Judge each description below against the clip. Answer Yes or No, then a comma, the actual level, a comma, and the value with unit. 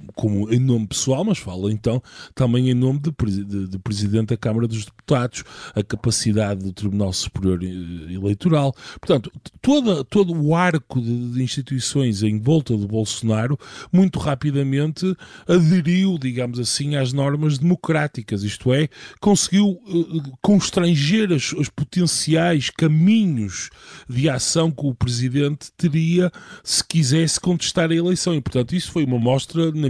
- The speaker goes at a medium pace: Yes, average, 145 wpm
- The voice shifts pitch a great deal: Yes, wide, 6.0 semitones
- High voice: No, medium, 140 Hz